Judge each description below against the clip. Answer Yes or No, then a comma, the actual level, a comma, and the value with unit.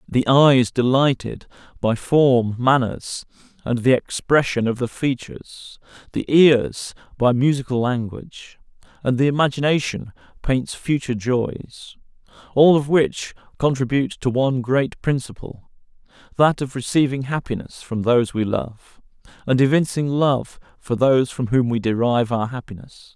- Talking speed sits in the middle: No, slow, 130 wpm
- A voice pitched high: No, low, 130 Hz